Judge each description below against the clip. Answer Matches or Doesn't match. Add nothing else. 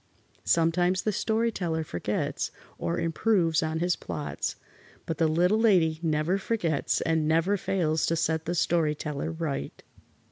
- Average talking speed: Matches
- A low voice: Doesn't match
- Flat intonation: Matches